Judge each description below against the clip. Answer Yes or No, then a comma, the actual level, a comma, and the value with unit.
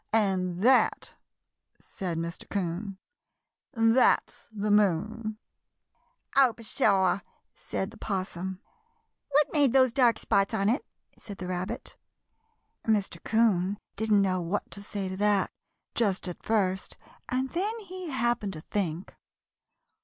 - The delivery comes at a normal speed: No, slow, 125 wpm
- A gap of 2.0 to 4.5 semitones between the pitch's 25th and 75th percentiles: Yes, average, 3.5 semitones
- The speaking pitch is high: Yes, high, 205 Hz